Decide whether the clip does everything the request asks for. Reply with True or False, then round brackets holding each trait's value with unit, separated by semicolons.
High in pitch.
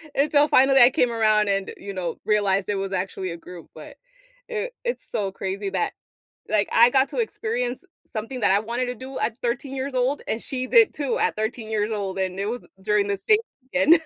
True (225 Hz)